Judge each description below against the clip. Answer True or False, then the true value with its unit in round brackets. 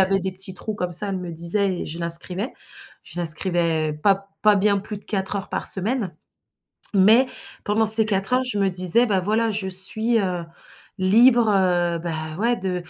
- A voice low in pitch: False (190 Hz)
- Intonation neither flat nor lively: True (3.2 semitones)